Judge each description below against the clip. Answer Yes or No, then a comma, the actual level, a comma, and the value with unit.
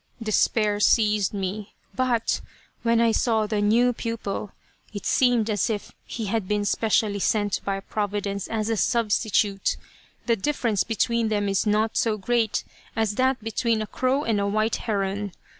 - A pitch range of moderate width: No, narrow, 2.0 semitones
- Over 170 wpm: No, average, 160 wpm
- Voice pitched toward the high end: Yes, high, 215 Hz